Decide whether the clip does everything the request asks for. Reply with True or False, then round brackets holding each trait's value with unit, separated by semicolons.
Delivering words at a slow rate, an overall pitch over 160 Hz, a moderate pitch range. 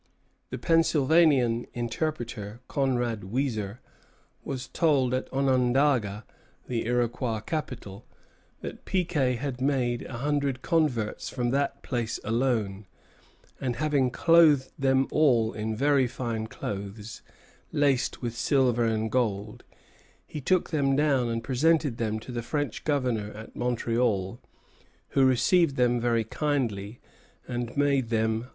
False (130 wpm; 125 Hz; 3.6 semitones)